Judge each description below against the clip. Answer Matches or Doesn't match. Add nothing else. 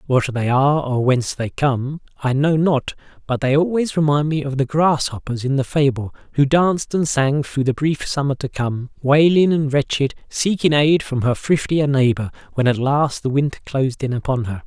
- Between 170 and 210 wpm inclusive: Matches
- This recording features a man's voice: Matches